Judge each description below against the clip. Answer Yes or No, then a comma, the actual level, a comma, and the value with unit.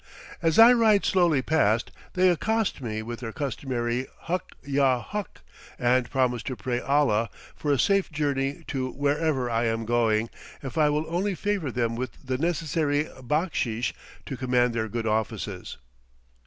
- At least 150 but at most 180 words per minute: Yes, average, 155 wpm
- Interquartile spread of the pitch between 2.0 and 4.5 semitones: No, average, 5.0 semitones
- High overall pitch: No, low, 135 Hz